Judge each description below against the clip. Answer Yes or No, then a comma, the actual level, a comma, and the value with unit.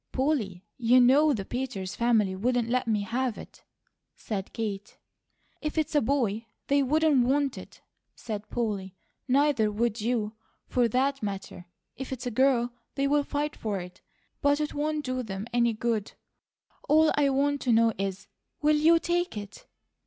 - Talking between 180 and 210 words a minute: No, average, 160 wpm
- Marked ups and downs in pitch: No, average, 5.0 semitones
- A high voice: Yes, high, 245 Hz